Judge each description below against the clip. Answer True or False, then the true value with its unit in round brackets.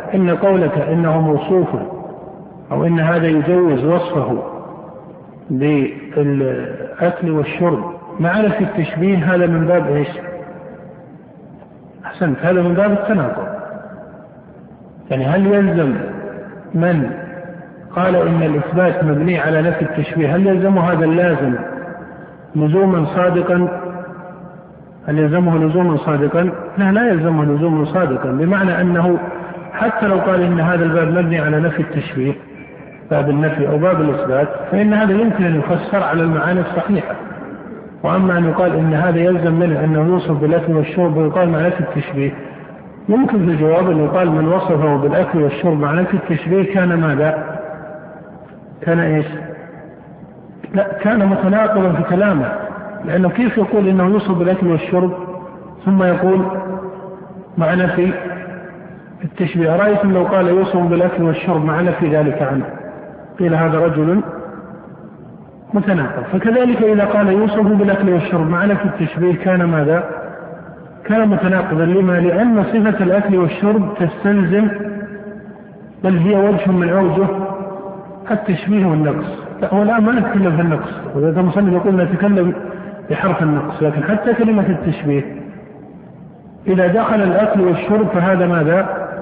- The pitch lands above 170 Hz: True (180 Hz)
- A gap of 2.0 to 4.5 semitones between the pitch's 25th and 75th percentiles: True (2.9 semitones)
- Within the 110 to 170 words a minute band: True (125 wpm)